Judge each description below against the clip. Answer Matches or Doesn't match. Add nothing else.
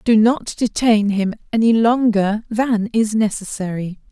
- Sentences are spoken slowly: Matches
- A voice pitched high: Matches